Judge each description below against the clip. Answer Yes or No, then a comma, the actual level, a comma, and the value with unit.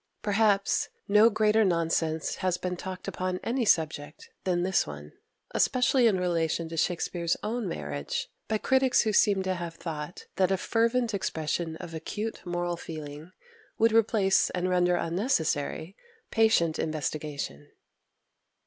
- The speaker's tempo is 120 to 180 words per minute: Yes, slow, 135 wpm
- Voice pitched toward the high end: No, medium, 180 Hz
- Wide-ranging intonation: No, average, 4.5 semitones